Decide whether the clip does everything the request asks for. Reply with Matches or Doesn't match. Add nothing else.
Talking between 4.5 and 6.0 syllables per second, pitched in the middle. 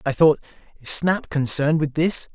Matches